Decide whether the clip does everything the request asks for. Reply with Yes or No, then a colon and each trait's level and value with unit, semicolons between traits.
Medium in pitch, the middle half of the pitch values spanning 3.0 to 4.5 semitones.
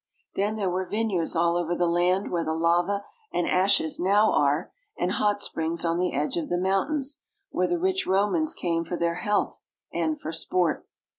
Yes: medium, 180 Hz; average, 3.3 semitones